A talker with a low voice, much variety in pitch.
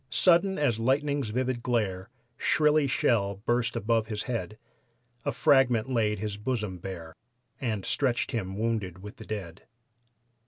No: low, 115 Hz; average, 4.0 semitones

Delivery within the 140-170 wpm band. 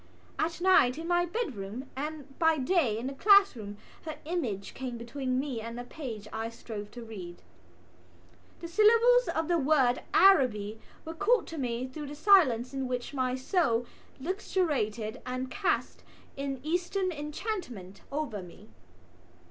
Yes: average, 150 wpm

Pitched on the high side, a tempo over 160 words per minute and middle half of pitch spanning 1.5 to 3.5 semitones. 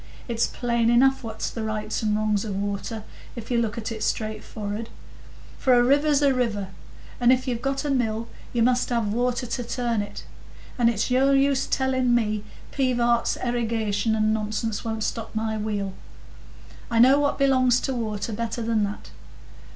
Yes: high, 230 Hz; average, 180 wpm; narrow, 2.5 semitones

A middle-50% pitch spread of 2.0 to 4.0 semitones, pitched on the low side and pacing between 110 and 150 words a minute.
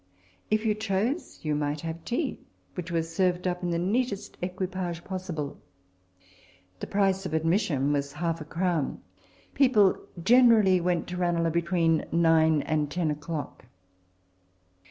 No: average, 3.1 semitones; medium, 175 Hz; average, 140 wpm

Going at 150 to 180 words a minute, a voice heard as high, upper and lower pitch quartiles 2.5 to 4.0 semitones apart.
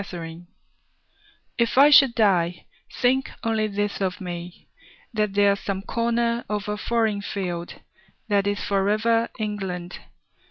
No: slow, 135 wpm; high, 205 Hz; average, 3.1 semitones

